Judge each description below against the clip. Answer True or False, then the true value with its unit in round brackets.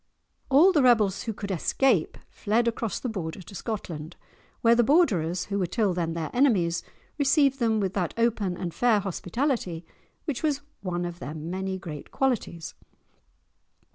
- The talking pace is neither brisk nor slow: True (160 wpm)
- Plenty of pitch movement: True (5.7 semitones)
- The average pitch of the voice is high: True (200 Hz)